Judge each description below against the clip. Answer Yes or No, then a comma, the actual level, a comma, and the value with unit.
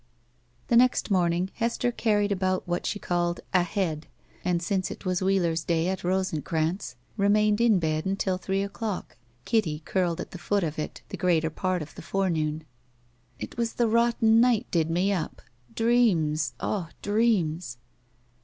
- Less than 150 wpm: No, average, 160 wpm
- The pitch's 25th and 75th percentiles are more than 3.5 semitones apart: Yes, average, 3.9 semitones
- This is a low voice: No, medium, 185 Hz